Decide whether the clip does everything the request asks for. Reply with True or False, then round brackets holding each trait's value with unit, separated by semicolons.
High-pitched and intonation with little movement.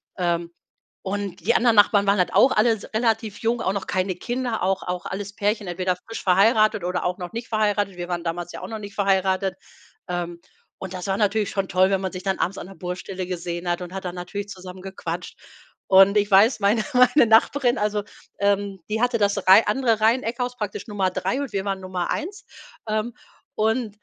False (200 Hz; 3.0 semitones)